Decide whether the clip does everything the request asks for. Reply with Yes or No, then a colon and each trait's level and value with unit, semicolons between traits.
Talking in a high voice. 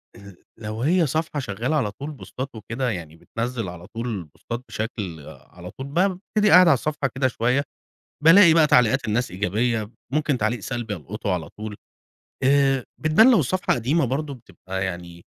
No: low, 120 Hz